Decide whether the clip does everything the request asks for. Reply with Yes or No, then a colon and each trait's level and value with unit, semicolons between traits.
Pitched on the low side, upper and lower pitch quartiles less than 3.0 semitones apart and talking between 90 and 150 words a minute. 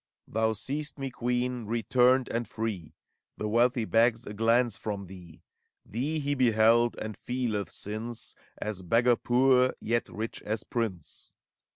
Yes: low, 115 Hz; narrow, 2.5 semitones; average, 140 wpm